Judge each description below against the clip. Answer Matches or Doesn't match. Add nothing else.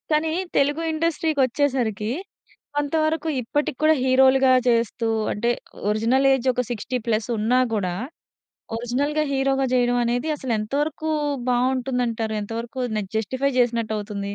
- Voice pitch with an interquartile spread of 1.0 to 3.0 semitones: Doesn't match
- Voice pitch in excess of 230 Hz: Matches